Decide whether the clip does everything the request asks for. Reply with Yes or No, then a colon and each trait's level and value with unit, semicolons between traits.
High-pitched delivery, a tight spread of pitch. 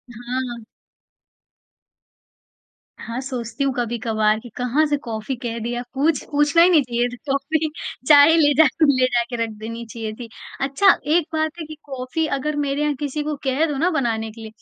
No: very high, 265 Hz; average, 3.9 semitones